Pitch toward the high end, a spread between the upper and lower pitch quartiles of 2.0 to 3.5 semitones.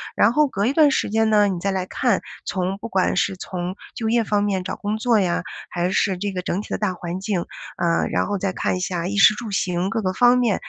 Yes: high, 195 Hz; average, 3.1 semitones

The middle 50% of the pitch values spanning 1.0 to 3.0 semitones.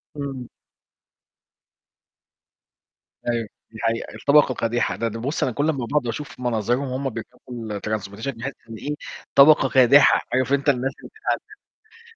No: average, 3.4 semitones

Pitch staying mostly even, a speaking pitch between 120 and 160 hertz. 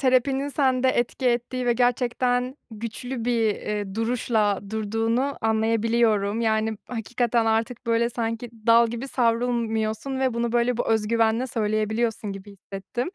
No: narrow, 1.9 semitones; high, 230 Hz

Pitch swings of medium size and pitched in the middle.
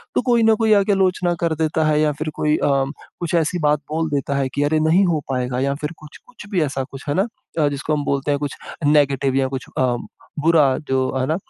Yes: average, 3.3 semitones; medium, 150 Hz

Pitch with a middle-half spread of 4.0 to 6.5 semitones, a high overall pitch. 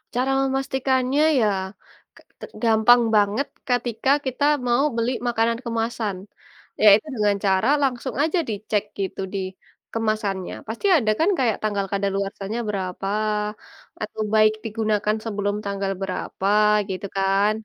No: average, 3.2 semitones; high, 215 Hz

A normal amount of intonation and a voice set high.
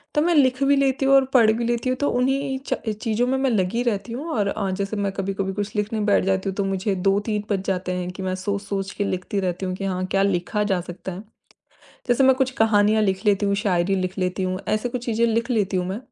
Yes: average, 3.7 semitones; high, 205 Hz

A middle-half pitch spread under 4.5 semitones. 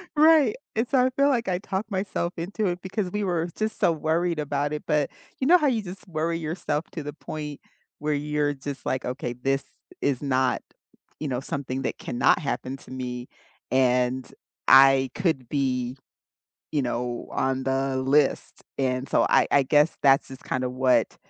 No: average, 5.1 semitones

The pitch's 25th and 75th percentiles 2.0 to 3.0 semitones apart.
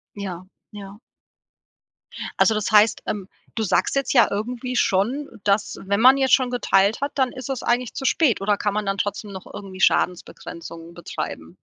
No: average, 4.2 semitones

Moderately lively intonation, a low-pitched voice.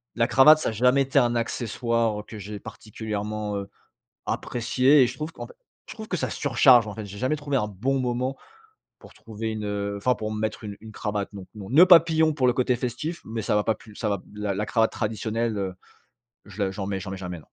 Yes: average, 3.6 semitones; low, 110 Hz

